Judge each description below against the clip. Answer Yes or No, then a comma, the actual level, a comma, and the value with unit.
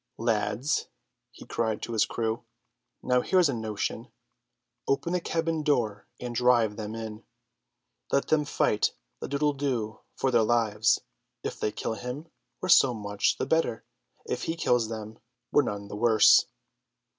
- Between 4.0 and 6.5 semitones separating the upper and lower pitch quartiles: Yes, average, 4.3 semitones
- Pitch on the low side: Yes, low, 115 Hz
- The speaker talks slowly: No, average, 155 wpm